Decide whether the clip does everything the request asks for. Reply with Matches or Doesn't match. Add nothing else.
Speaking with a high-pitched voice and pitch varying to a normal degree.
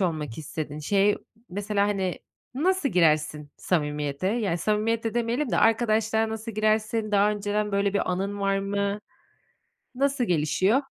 Matches